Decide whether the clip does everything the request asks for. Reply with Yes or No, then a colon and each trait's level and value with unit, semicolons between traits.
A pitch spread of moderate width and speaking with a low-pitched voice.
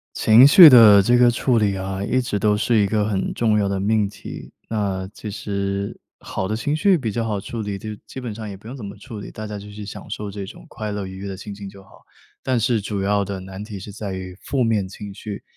No: narrow, 2.3 semitones; low, 105 Hz